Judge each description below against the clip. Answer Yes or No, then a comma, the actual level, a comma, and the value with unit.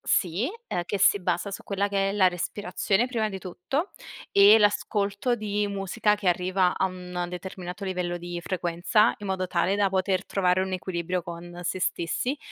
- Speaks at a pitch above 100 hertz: Yes, high, 190 Hz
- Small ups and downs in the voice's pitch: Yes, narrow, 2.3 semitones